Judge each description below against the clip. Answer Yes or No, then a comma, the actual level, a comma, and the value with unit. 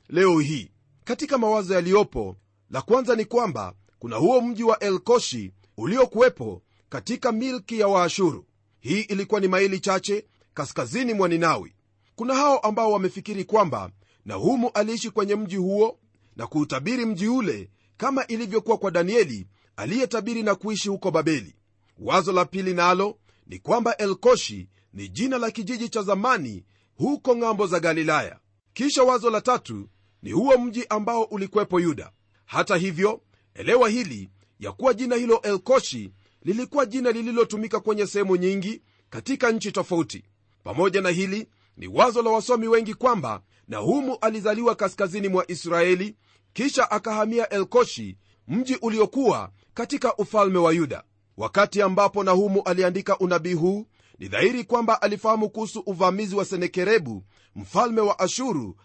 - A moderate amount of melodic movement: No, wide, 6.4 semitones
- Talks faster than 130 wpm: Yes, fast, 140 wpm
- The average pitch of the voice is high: Yes, high, 200 Hz